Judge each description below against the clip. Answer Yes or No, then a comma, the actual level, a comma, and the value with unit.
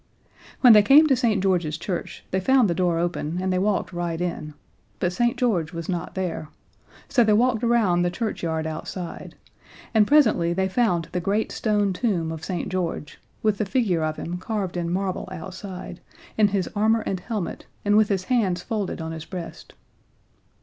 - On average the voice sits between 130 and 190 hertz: Yes, medium, 185 Hz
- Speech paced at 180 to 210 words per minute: Yes, average, 185 wpm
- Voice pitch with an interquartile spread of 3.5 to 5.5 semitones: Yes, average, 3.9 semitones